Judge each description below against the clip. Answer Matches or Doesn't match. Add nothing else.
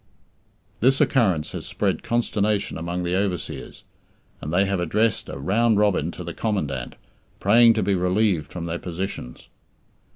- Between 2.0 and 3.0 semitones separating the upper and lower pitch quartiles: Doesn't match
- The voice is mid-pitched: Doesn't match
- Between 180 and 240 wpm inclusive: Doesn't match